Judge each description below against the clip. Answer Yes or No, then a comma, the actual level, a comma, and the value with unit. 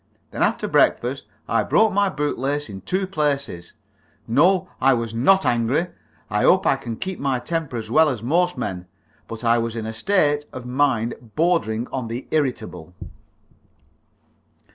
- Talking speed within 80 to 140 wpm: No, average, 165 wpm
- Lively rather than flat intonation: Yes, wide, 5.9 semitones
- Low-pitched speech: Yes, low, 130 Hz